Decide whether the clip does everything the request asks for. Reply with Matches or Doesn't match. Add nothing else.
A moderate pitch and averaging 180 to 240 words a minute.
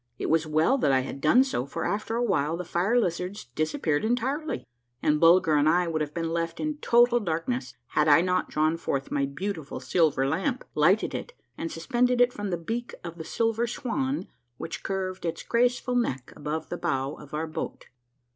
Matches